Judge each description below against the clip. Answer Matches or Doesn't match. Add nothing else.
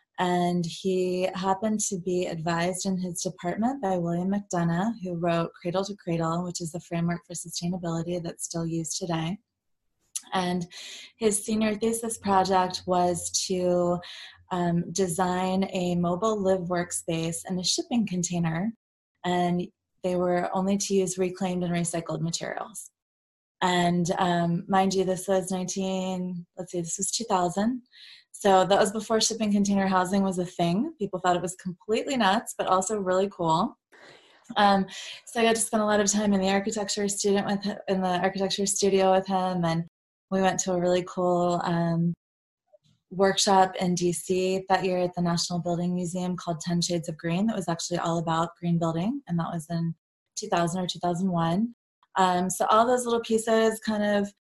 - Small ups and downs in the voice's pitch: Matches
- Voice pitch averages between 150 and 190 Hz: Matches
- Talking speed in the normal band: Matches